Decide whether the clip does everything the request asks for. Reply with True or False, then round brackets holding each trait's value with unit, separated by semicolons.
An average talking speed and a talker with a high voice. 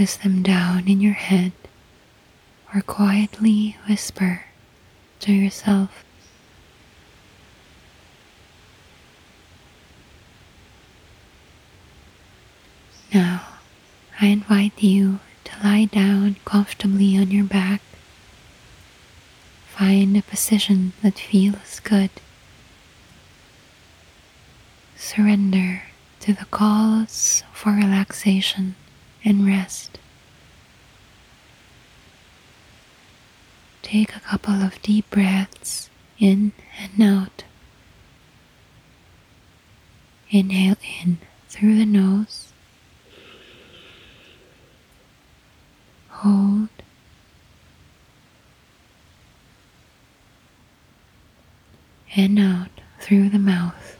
False (60 wpm; 200 Hz)